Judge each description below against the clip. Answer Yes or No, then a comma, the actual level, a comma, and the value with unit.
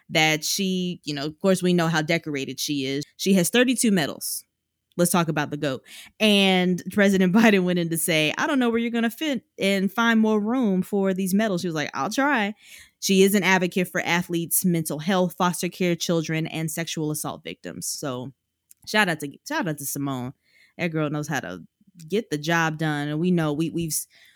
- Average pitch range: Yes, average, 4.2 semitones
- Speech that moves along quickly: Yes, fast, 210 wpm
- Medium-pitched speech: Yes, medium, 175 Hz